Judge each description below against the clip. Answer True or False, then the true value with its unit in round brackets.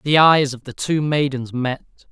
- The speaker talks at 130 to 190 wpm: False (200 wpm)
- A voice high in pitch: False (140 Hz)